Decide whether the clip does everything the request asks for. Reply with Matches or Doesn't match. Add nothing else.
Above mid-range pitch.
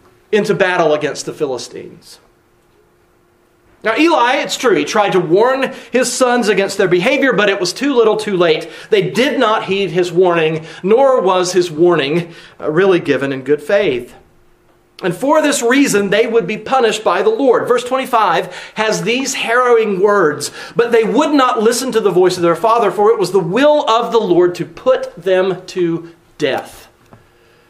Matches